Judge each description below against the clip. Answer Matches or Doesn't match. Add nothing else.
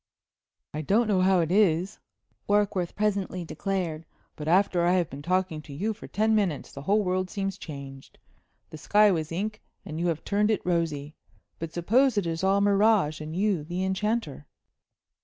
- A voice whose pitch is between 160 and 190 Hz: Matches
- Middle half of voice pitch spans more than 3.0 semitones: Matches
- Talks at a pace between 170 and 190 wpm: Matches